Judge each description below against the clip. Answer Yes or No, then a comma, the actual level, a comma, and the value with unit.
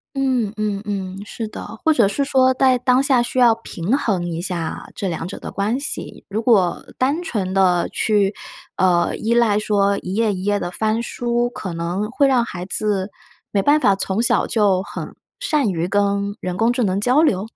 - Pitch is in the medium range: No, high, 210 Hz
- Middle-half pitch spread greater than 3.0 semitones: Yes, average, 4.2 semitones